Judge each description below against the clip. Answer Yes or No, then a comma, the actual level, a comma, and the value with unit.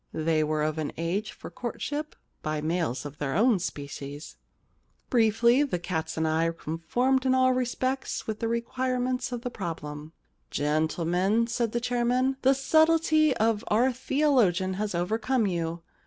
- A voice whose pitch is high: Yes, high, 215 Hz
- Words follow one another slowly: No, average, 165 wpm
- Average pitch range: No, wide, 7.7 semitones